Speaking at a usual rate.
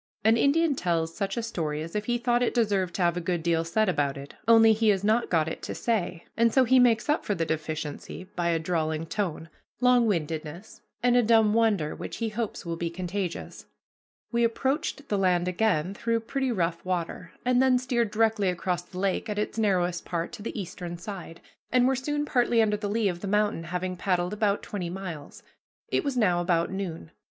No: fast, 210 wpm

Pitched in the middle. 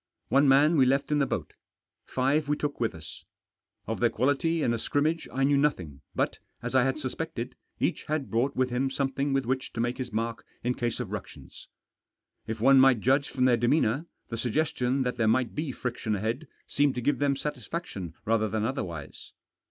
No: low, 130 Hz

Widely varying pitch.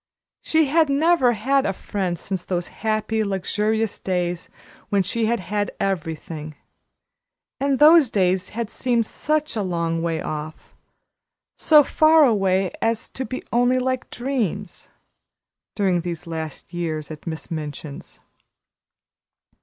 Yes: wide, 6.4 semitones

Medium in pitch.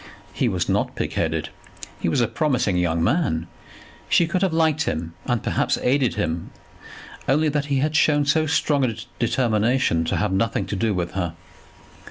No: low, 125 Hz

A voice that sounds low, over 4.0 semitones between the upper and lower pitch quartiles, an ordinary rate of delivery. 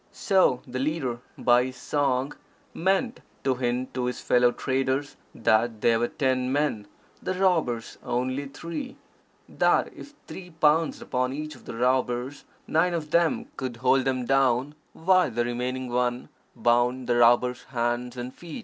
No: low, 130 Hz; average, 3.4 semitones; average, 155 wpm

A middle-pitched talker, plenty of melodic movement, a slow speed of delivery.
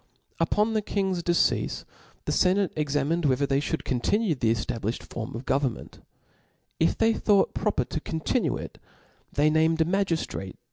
No: medium, 160 Hz; wide, 6.0 semitones; average, 155 wpm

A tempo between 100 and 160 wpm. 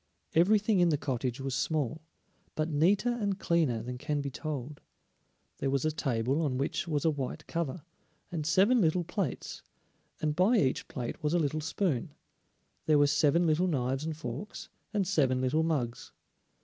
No: average, 170 wpm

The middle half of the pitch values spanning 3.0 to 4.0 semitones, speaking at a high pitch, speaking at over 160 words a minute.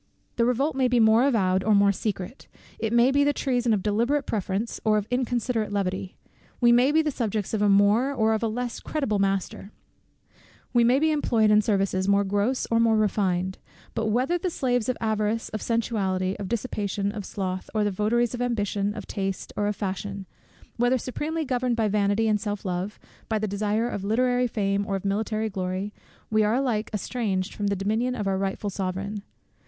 Yes: average, 3.3 semitones; high, 215 Hz; average, 195 wpm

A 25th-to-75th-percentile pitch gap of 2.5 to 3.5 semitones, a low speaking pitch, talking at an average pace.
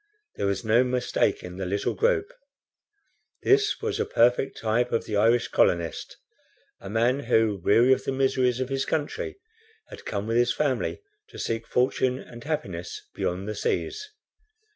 No: average, 4.2 semitones; low, 120 Hz; average, 160 wpm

